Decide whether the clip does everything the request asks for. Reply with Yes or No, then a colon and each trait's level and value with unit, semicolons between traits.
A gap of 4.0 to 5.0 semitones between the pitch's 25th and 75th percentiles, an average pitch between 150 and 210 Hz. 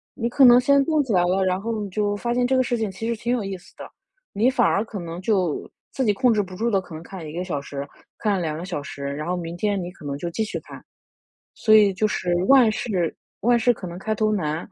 Yes: average, 4.6 semitones; high, 200 Hz